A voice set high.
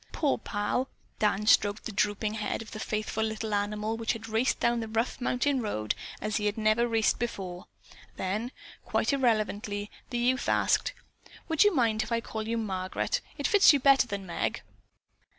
Yes: high, 220 Hz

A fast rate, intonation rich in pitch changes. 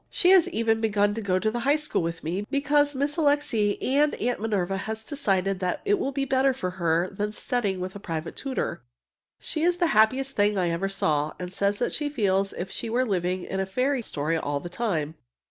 Yes: fast, 220 wpm; wide, 6.6 semitones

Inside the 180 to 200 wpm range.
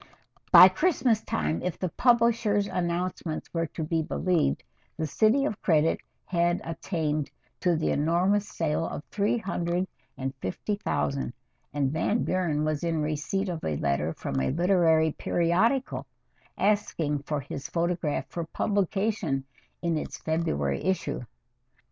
No: slow, 135 wpm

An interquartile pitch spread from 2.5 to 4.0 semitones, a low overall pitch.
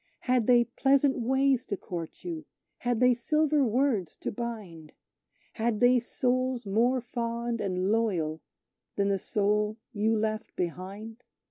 No: average, 3.6 semitones; high, 230 Hz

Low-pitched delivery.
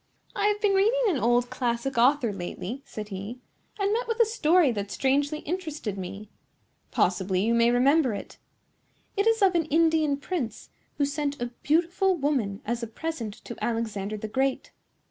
No: very high, 270 Hz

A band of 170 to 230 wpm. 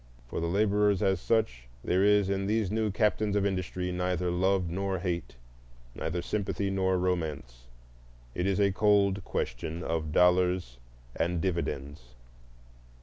No: average, 140 wpm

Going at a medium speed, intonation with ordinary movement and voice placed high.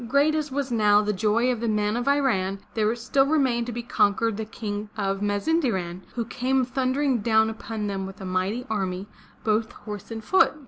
Yes: average, 195 wpm; average, 3.5 semitones; high, 220 Hz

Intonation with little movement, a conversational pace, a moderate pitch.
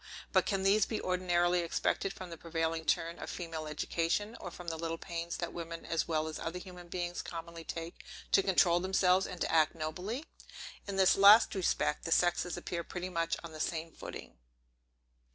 Yes: narrow, 1.8 semitones; average, 190 wpm; medium, 175 Hz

